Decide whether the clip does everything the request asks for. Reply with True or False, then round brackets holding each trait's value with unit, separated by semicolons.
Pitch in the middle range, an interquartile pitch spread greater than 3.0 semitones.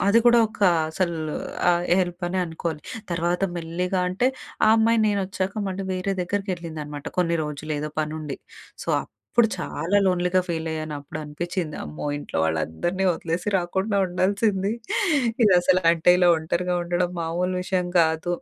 False (175 Hz; 2.7 semitones)